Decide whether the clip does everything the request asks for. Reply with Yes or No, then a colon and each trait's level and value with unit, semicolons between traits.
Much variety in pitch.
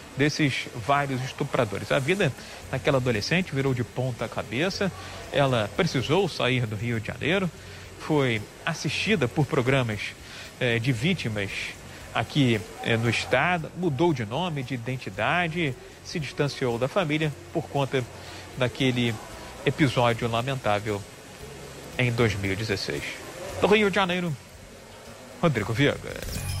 No: average, 5.0 semitones